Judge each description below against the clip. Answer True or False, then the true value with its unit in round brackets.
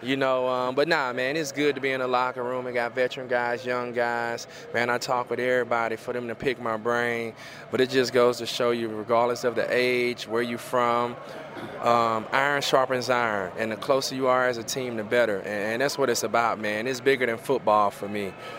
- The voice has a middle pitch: False (120 Hz)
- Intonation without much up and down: True (1.5 semitones)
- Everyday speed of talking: False (230 wpm)